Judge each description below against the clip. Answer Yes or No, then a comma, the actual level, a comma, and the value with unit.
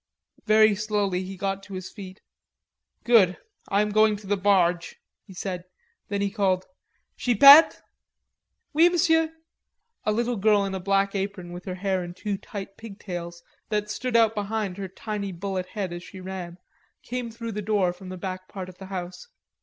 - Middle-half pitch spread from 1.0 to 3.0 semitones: Yes, narrow, 2.5 semitones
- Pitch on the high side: Yes, high, 195 Hz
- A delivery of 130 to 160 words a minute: No, average, 175 wpm